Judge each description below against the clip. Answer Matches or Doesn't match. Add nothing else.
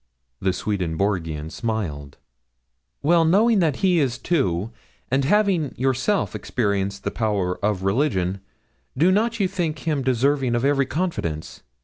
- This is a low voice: Matches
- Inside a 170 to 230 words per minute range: Doesn't match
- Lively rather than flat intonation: Matches